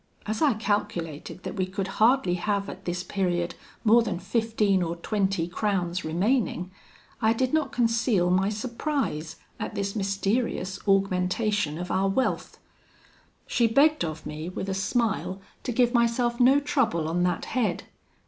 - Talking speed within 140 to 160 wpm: Yes, average, 150 wpm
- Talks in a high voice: Yes, high, 200 Hz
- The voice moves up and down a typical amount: Yes, average, 4.4 semitones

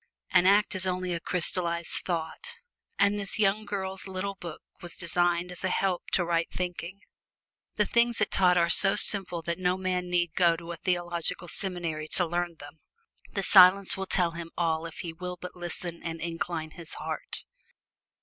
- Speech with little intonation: Yes, narrow, 1.9 semitones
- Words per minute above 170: Yes, average, 180 wpm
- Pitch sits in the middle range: Yes, medium, 175 Hz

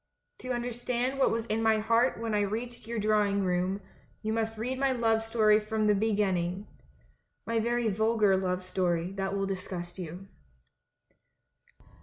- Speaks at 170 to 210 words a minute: No, average, 160 wpm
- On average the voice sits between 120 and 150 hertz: No, high, 215 Hz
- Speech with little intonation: No, average, 3.0 semitones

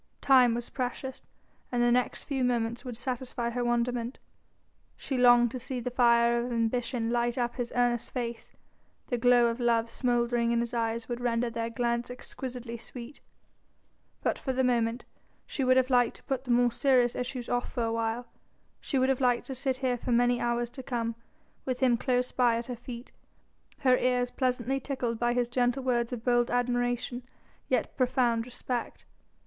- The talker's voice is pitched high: Yes, high, 245 Hz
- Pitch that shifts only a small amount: Yes, narrow, 1.1 semitones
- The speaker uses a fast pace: No, average, 185 wpm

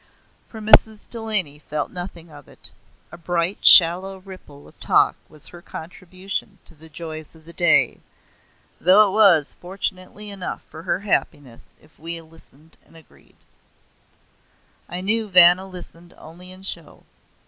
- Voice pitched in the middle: Yes, medium, 175 Hz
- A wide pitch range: No, average, 3.0 semitones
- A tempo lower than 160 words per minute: Yes, average, 145 wpm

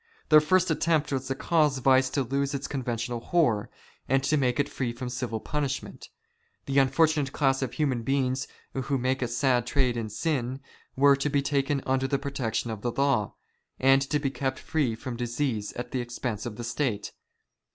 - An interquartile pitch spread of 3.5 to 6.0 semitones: No, narrow, 2.4 semitones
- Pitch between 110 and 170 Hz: Yes, low, 135 Hz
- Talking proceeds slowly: No, average, 195 wpm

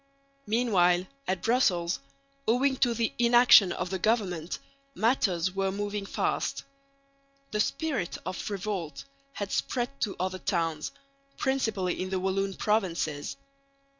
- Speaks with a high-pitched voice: Yes, high, 195 Hz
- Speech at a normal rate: No, slow, 120 wpm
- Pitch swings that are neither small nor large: Yes, average, 4.2 semitones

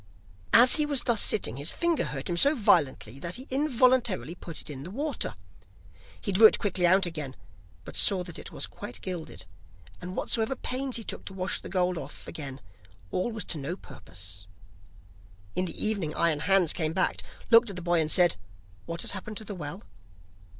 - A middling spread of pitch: No, wide, 6.0 semitones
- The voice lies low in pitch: No, medium, 180 Hz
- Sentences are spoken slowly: No, average, 195 wpm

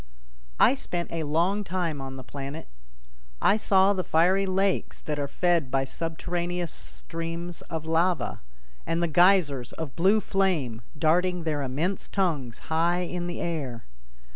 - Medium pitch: Yes, medium, 170 Hz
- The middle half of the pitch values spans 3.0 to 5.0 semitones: Yes, average, 3.3 semitones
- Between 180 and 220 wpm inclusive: No, average, 145 wpm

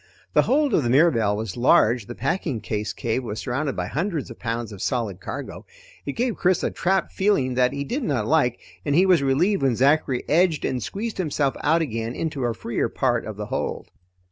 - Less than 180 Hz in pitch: Yes, low, 135 Hz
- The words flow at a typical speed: No, fast, 210 wpm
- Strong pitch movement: Yes, wide, 6.0 semitones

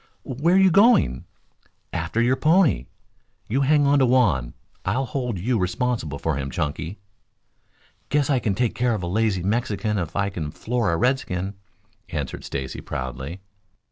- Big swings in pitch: Yes, wide, 7.3 semitones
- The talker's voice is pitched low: Yes, low, 110 Hz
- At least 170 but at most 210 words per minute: No, average, 160 wpm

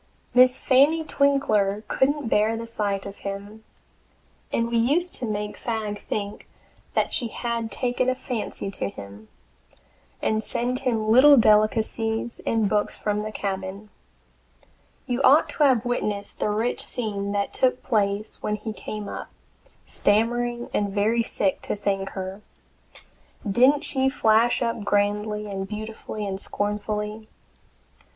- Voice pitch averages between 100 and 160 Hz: No, high, 215 Hz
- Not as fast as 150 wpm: Yes, average, 140 wpm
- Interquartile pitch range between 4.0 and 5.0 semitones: No, average, 2.9 semitones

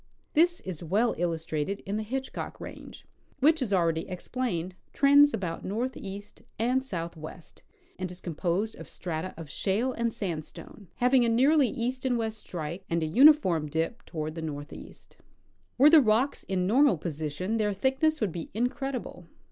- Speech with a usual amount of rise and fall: No, wide, 7.2 semitones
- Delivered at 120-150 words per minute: No, average, 160 wpm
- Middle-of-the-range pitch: No, high, 205 Hz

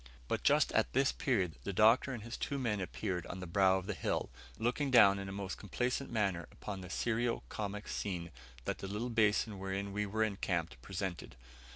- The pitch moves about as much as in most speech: Yes, average, 3.1 semitones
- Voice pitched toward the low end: Yes, low, 100 Hz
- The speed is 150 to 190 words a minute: No, average, 200 wpm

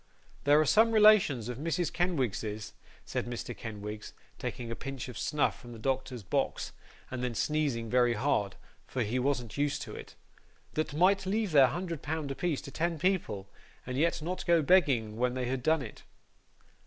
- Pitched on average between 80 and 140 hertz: Yes, low, 135 Hz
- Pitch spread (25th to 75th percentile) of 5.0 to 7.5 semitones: Yes, wide, 5.5 semitones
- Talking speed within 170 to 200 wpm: Yes, average, 180 wpm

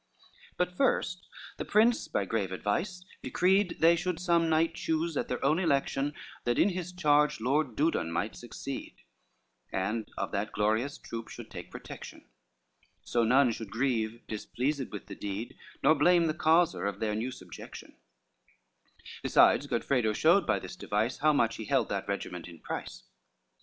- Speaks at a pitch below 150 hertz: Yes, medium, 140 Hz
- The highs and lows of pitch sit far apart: Yes, wide, 7.2 semitones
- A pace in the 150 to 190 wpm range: Yes, average, 165 wpm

